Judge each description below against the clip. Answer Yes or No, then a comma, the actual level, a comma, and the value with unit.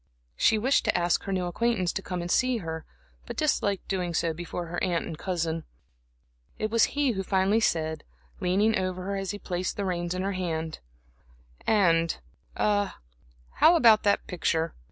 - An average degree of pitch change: Yes, average, 3.1 semitones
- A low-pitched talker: No, medium, 185 Hz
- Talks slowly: No, average, 175 wpm